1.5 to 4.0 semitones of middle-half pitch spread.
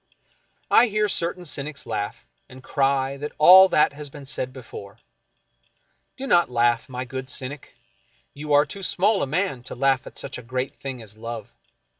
Yes: average, 3.3 semitones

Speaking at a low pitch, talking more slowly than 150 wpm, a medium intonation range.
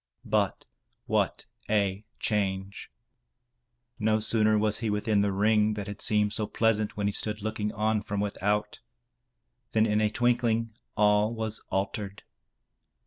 No: low, 105 Hz; average, 140 wpm; narrow, 1.1 semitones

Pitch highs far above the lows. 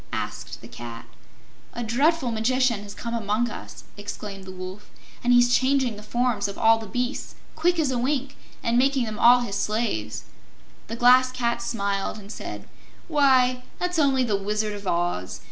No: average, 3.8 semitones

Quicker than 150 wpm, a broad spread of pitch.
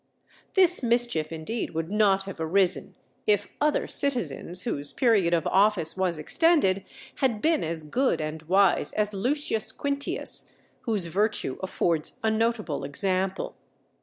No: slow, 135 wpm; wide, 5.9 semitones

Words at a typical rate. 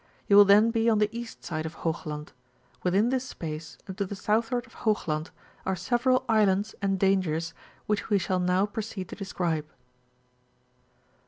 Yes: average, 170 wpm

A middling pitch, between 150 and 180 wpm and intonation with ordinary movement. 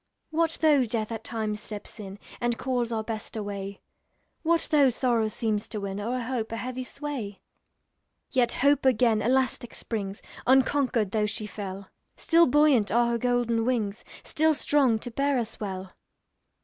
No: high, 235 Hz; average, 160 wpm; average, 3.6 semitones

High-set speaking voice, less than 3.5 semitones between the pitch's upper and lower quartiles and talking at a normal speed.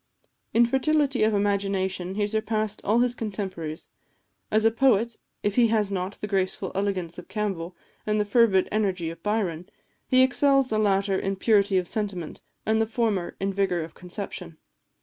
Yes: high, 205 Hz; average, 2.8 semitones; average, 170 wpm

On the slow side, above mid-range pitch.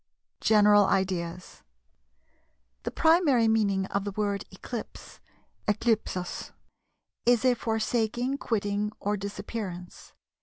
Yes: slow, 90 wpm; high, 210 Hz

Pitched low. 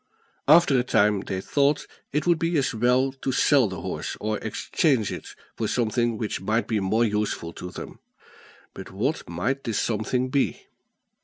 Yes: low, 120 Hz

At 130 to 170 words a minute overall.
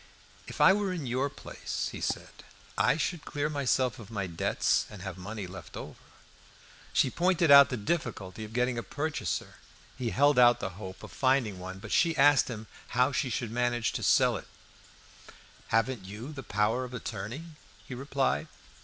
No: average, 180 wpm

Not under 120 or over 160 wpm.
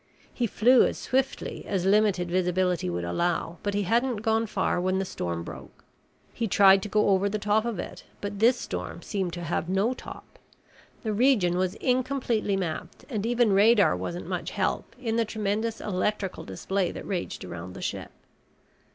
No: average, 175 wpm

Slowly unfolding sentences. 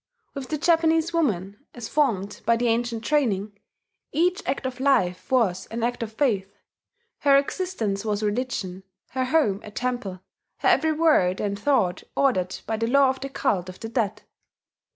No: average, 170 wpm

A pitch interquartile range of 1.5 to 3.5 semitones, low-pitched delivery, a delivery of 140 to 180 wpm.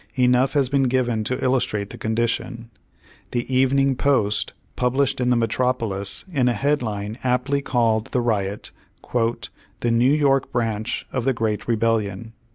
Yes: average, 2.7 semitones; low, 120 Hz; average, 145 wpm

